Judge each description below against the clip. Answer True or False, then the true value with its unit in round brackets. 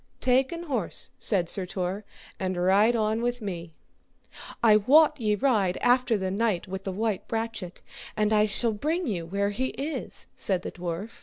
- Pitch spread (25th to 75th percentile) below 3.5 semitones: False (4.4 semitones)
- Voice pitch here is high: True (210 Hz)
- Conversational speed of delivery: True (175 wpm)